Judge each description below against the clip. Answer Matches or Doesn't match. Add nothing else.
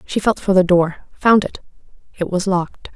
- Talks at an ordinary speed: Matches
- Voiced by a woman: Matches